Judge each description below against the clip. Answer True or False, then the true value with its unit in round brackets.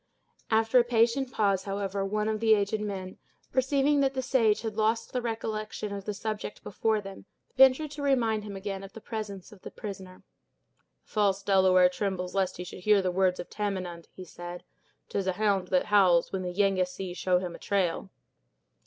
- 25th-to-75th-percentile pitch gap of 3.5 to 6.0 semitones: False (2.9 semitones)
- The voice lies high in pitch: True (200 Hz)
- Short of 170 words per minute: False (190 wpm)